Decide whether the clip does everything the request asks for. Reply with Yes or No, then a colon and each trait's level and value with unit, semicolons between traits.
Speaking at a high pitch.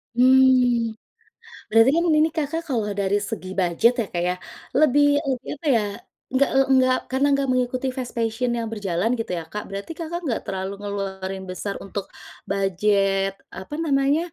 Yes: high, 230 Hz